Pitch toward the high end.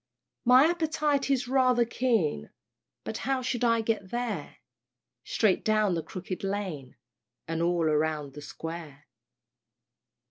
Yes: high, 205 Hz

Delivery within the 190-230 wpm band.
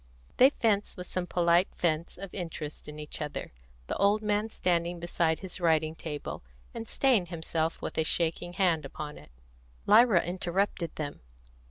No: average, 160 wpm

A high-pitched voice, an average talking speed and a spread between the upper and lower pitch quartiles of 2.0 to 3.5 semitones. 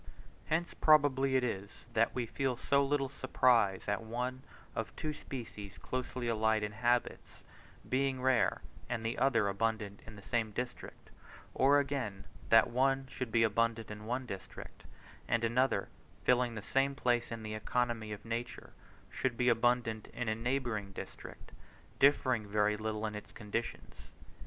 No: low, 120 Hz; average, 155 wpm; average, 2.9 semitones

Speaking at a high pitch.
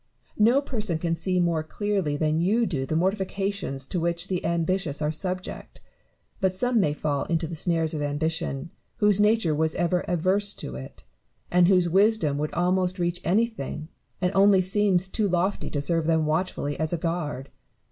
No: medium, 175 Hz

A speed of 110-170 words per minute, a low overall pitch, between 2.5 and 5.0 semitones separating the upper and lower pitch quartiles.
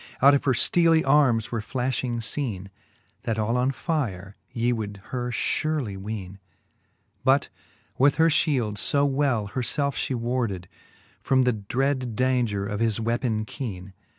Yes: average, 150 wpm; low, 120 Hz; average, 4.1 semitones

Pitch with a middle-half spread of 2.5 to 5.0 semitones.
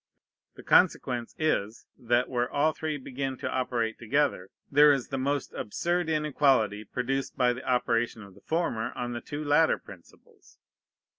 Yes: average, 3.7 semitones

